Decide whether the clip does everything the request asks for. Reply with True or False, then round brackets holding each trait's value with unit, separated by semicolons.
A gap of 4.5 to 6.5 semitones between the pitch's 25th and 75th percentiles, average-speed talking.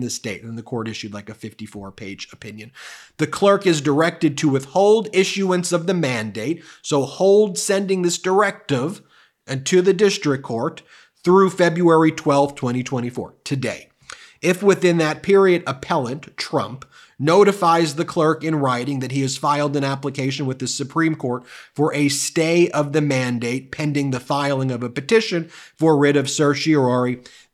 True (5.0 semitones; 160 wpm)